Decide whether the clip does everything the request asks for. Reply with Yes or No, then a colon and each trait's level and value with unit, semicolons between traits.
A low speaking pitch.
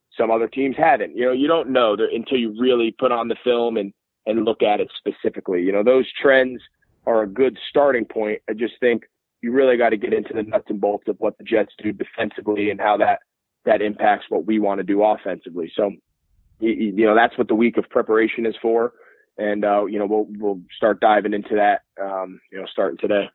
Yes: low, 110 Hz